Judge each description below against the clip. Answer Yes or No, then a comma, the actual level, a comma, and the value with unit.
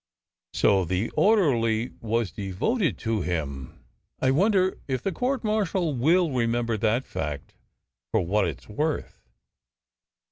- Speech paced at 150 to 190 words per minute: No, slow, 135 wpm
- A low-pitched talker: Yes, low, 120 Hz